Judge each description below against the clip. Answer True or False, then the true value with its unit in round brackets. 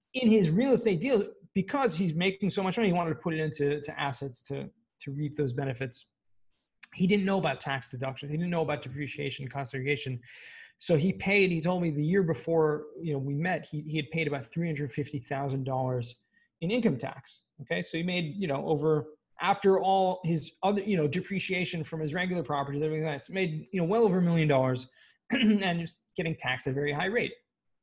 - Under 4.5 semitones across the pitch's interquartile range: False (4.9 semitones)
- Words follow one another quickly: True (210 wpm)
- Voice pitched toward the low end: False (160 Hz)